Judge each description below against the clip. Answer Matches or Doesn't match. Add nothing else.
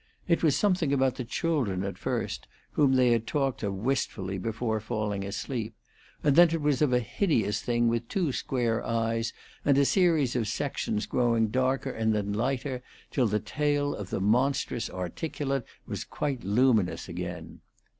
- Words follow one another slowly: Doesn't match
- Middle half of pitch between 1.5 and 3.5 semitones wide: Doesn't match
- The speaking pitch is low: Matches